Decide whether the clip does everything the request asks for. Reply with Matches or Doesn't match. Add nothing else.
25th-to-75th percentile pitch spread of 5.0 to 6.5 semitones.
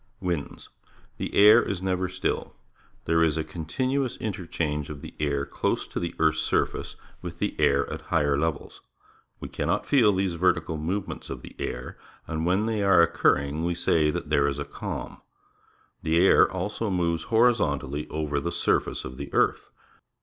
Doesn't match